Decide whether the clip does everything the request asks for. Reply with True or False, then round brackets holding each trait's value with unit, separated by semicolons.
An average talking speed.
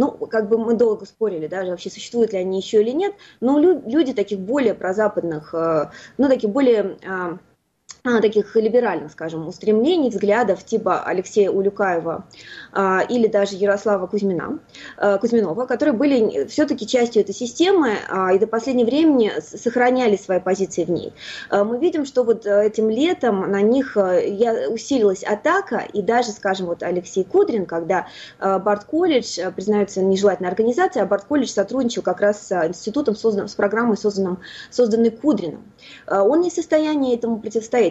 True (140 wpm)